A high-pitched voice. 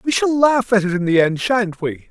Yes: high, 210 Hz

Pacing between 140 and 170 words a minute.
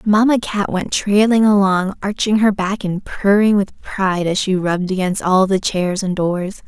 No: average, 190 wpm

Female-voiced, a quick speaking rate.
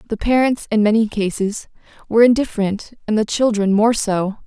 No: female; average, 160 wpm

